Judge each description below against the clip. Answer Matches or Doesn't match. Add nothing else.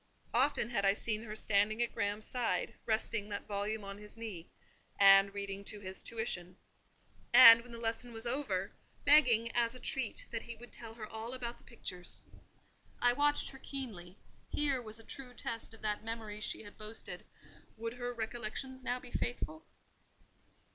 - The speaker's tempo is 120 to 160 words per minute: Doesn't match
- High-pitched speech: Matches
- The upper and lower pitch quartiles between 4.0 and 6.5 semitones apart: Doesn't match